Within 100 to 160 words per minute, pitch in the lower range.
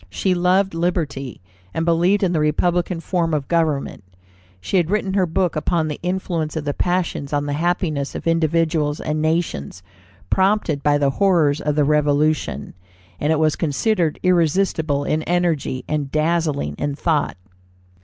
No: average, 155 wpm; medium, 160 Hz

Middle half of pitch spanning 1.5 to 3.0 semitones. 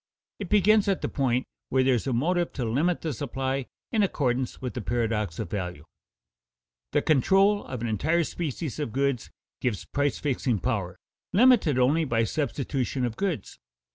No: wide, 5.6 semitones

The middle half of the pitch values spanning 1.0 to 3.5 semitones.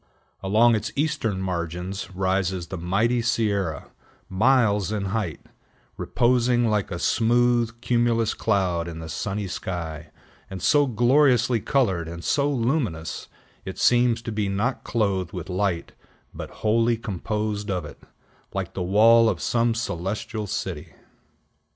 No: average, 4.1 semitones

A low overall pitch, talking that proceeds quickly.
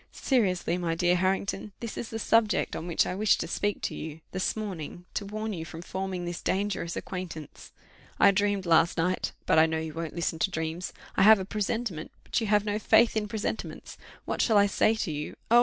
No: high, 190 Hz; fast, 215 wpm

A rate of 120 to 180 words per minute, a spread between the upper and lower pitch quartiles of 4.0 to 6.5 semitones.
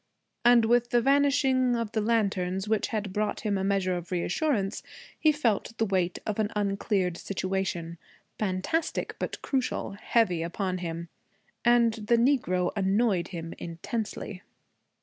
Yes: average, 140 wpm; average, 4.3 semitones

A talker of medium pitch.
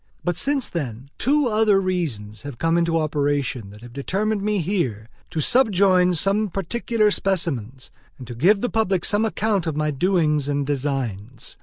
Yes: medium, 165 Hz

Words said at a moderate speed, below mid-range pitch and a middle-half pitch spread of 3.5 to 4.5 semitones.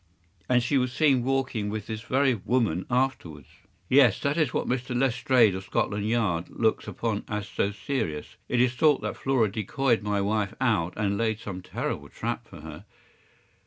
Yes: average, 180 wpm; low, 115 Hz; average, 4.0 semitones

